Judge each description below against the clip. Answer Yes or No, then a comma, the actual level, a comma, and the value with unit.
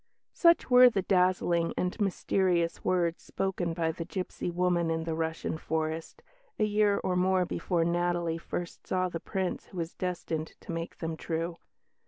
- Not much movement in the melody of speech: Yes, narrow, 2.0 semitones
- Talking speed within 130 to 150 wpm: No, average, 165 wpm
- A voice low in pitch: No, medium, 175 Hz